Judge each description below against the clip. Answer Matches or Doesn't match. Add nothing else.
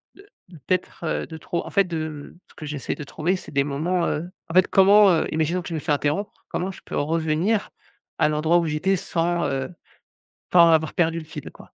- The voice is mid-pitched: Matches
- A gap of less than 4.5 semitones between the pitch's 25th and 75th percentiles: Matches